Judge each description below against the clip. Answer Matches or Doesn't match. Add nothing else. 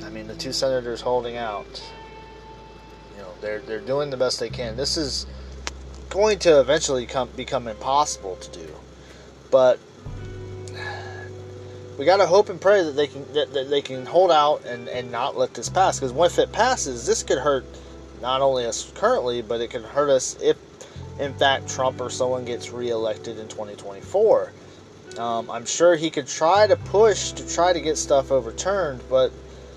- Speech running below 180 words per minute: Matches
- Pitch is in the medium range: Doesn't match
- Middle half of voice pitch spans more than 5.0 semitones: Matches